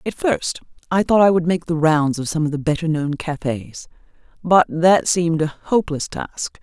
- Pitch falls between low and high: Yes, medium, 160 Hz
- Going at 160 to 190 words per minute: No, average, 200 wpm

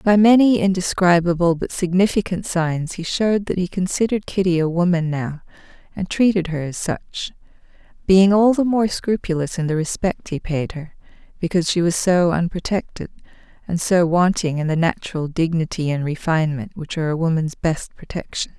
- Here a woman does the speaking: Yes, female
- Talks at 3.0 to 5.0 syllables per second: No, 5.3 syllables/s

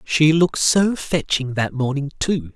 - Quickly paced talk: No, average, 165 wpm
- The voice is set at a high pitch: No, medium, 145 Hz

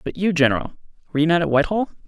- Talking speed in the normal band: No, fast, 230 wpm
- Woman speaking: No, male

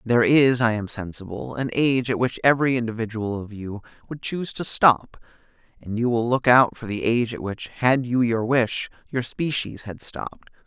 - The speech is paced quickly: No, average, 195 wpm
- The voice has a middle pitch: No, low, 120 Hz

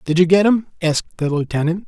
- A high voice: No, medium, 170 Hz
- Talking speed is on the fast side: Yes, fast, 225 wpm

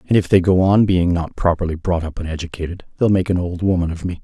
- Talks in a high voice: No, very low, 90 Hz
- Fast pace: Yes, fast, 270 wpm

